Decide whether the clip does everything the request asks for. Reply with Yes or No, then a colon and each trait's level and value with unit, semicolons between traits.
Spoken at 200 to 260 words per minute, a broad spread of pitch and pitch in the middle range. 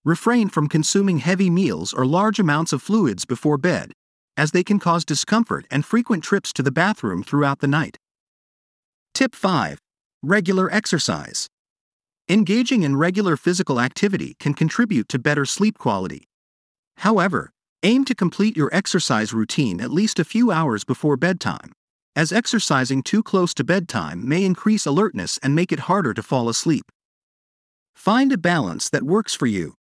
No: average, 155 wpm; wide, 6.2 semitones; medium, 175 Hz